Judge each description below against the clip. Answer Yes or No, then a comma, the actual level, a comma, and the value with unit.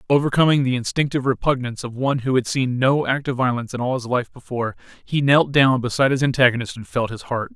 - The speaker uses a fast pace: Yes, fast, 220 wpm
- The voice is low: Yes, low, 130 Hz